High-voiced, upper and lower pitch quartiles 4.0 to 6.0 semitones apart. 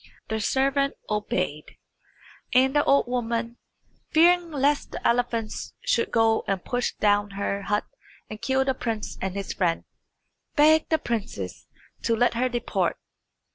Yes: high, 235 Hz; average, 4.5 semitones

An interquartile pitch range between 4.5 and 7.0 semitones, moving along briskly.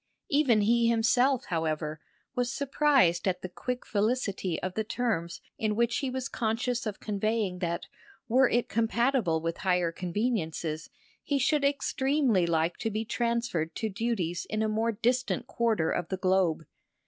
No: wide, 5.4 semitones; average, 155 wpm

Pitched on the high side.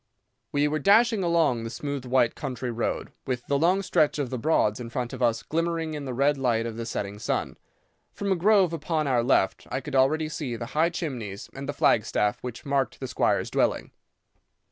No: low, 135 Hz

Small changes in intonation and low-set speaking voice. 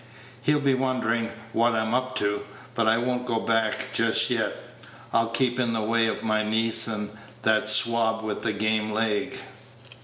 Yes: narrow, 1.5 semitones; low, 115 Hz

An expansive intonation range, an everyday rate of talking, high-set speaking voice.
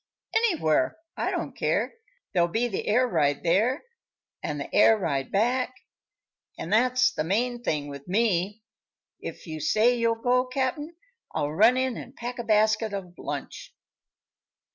Yes: wide, 6.3 semitones; average, 150 wpm; high, 220 Hz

